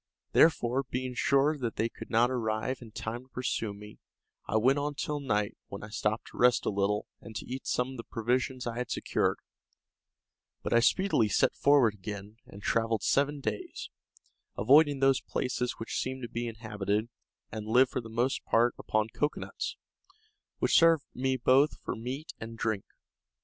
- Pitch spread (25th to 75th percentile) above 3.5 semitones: No, average, 3.2 semitones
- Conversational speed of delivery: Yes, average, 175 wpm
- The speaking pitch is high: No, low, 120 Hz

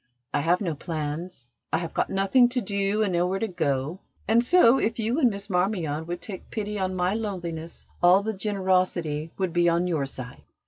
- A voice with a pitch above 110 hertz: Yes, medium, 185 Hz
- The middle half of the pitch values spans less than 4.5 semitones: Yes, average, 3.8 semitones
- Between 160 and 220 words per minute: Yes, average, 195 wpm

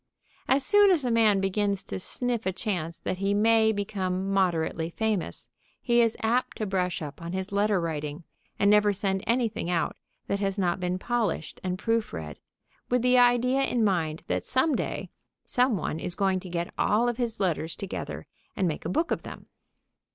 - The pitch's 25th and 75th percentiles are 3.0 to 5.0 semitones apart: Yes, average, 4.2 semitones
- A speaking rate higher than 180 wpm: Yes, average, 190 wpm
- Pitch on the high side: Yes, high, 200 Hz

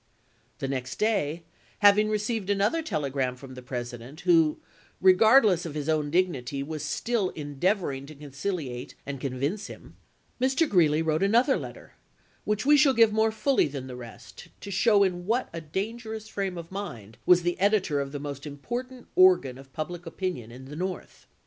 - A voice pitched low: No, medium, 175 Hz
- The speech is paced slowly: No, average, 175 wpm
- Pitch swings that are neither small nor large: No, wide, 7.1 semitones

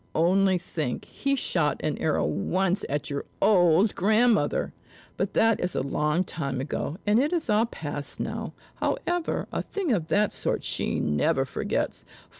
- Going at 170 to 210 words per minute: No, average, 160 wpm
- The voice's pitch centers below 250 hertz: Yes, medium, 185 Hz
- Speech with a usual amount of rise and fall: No, wide, 6.5 semitones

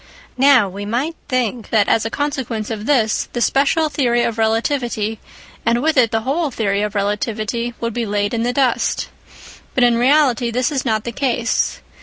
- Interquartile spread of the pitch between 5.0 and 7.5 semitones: No, average, 2.9 semitones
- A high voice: Yes, high, 235 Hz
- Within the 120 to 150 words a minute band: No, average, 185 wpm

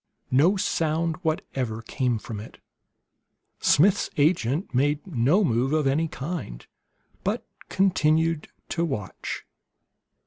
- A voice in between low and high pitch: Yes, medium, 150 Hz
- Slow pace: Yes, slow, 105 wpm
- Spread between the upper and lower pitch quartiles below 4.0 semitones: No, average, 4.5 semitones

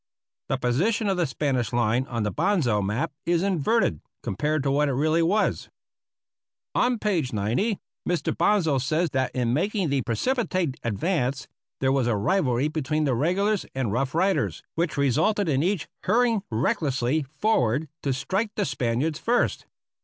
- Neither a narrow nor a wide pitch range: No, wide, 6.8 semitones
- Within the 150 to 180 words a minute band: Yes, average, 155 wpm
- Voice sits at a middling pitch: Yes, medium, 150 Hz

